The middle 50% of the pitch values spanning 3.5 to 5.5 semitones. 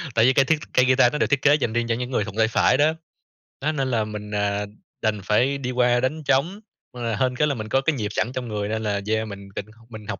Yes: average, 3.8 semitones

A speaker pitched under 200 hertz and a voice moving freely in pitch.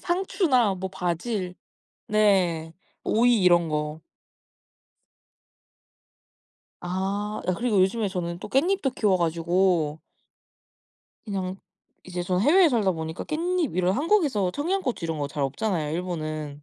Yes: high, 190 Hz; wide, 6.0 semitones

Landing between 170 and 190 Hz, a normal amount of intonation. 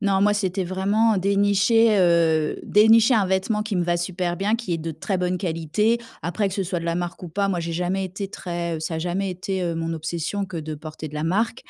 Yes: medium, 185 Hz; average, 3.1 semitones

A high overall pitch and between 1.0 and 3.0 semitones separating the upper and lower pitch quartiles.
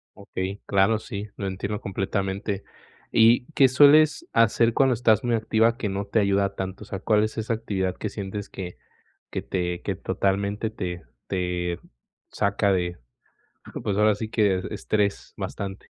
No: low, 100 Hz; narrow, 2.5 semitones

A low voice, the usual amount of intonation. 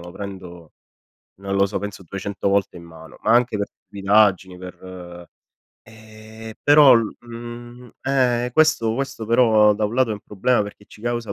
Yes: low, 110 Hz; average, 3.4 semitones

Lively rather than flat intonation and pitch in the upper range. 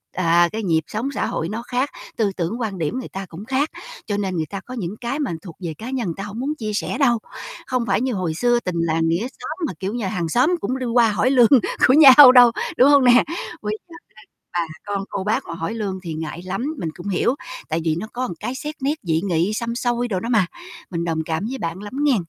Yes: wide, 6.3 semitones; high, 210 Hz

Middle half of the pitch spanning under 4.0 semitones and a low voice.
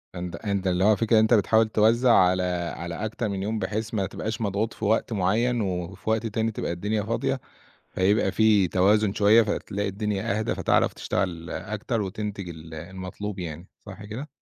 Yes: average, 2.9 semitones; low, 105 Hz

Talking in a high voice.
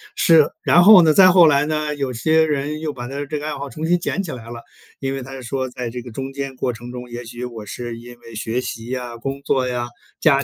No: low, 135 Hz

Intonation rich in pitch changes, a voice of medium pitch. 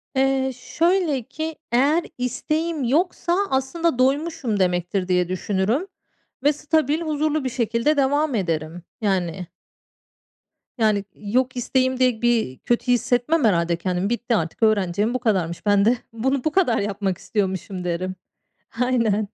No: wide, 6.2 semitones; high, 240 Hz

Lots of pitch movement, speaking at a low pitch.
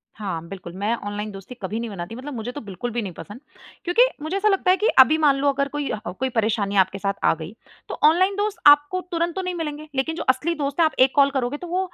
No: wide, 7.6 semitones; very high, 265 Hz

